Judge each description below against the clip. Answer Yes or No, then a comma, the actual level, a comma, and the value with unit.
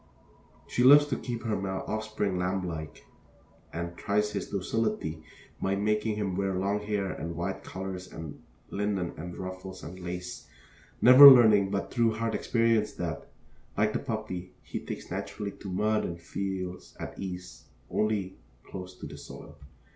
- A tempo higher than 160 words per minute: No, average, 155 wpm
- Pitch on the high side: No, very low, 95 Hz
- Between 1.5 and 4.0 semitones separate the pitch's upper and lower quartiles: Yes, average, 2.9 semitones